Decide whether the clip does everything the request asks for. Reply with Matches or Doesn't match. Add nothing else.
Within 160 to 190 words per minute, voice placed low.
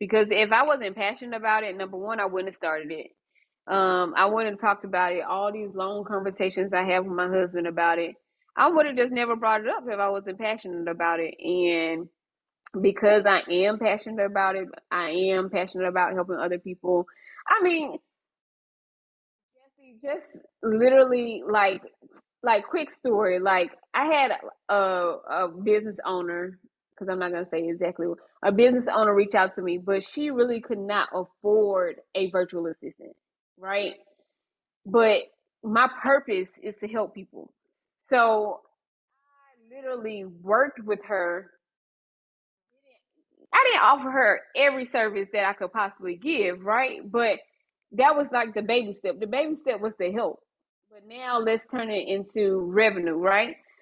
Doesn't match